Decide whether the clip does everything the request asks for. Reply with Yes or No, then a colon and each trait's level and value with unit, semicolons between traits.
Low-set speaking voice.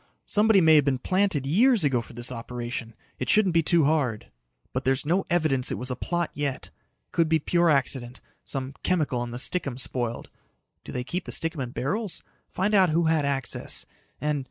No: medium, 145 Hz